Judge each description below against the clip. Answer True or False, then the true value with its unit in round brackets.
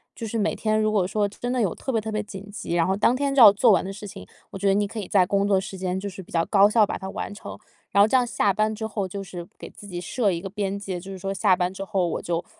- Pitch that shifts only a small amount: True (2.1 semitones)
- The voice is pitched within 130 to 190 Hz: False (200 Hz)